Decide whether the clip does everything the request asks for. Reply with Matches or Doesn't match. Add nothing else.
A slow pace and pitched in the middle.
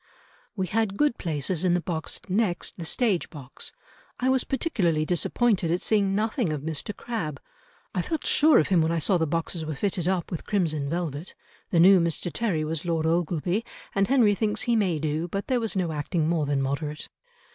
Doesn't match